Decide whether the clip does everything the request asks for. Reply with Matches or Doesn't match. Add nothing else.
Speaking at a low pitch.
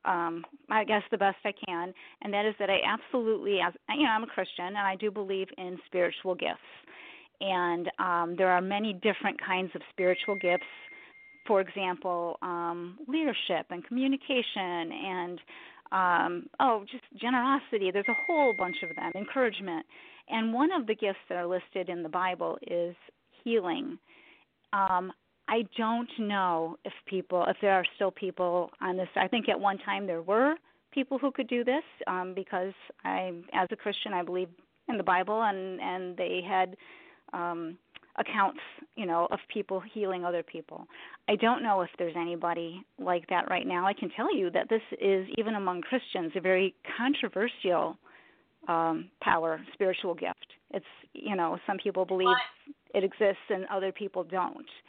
Doesn't match